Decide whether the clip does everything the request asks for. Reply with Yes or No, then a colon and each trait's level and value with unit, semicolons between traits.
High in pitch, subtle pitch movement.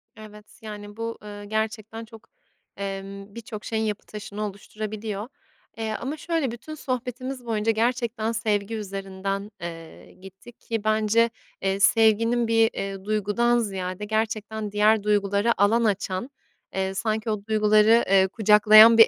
Yes: high, 215 Hz; narrow, 2.0 semitones